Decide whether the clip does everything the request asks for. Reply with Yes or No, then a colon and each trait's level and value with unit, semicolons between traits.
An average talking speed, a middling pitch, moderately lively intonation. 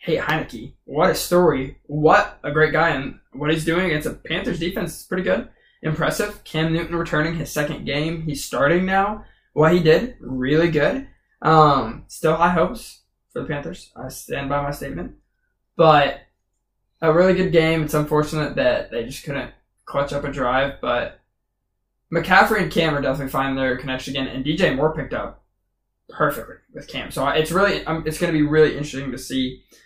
Yes: average, 185 wpm; medium, 155 Hz; average, 3.0 semitones